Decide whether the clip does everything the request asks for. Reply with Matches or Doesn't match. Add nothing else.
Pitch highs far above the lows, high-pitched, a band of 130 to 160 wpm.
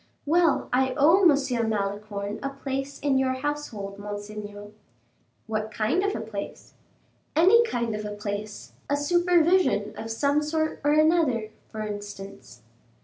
Matches